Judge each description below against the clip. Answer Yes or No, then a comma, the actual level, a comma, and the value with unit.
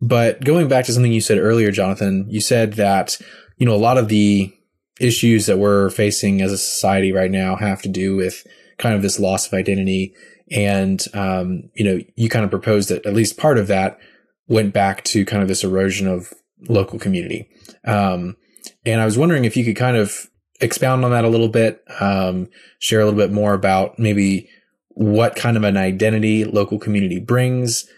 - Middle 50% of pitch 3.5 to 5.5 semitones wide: No, average, 3.0 semitones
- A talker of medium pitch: No, low, 105 Hz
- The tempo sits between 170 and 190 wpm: No, average, 200 wpm